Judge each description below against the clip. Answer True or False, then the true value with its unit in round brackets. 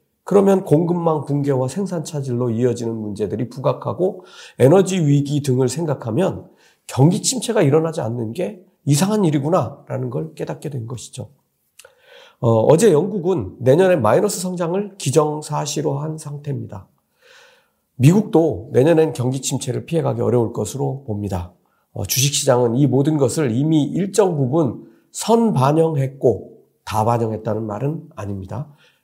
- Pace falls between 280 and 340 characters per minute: True (310 characters per minute)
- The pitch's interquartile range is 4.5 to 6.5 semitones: True (5.6 semitones)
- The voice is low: False (145 Hz)